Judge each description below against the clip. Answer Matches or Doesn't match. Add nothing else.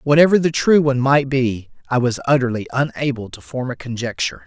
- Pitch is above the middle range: Doesn't match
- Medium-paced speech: Matches